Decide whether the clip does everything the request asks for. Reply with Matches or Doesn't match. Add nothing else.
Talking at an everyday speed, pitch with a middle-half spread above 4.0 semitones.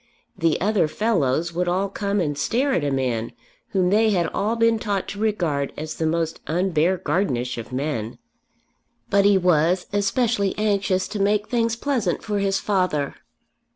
Matches